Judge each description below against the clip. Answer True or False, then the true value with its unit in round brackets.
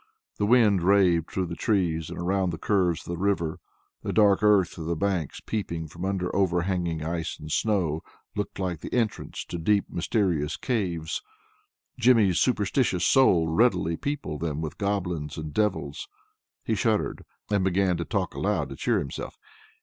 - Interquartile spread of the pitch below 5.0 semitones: True (3.7 semitones)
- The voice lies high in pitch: False (90 Hz)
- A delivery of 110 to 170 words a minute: True (165 wpm)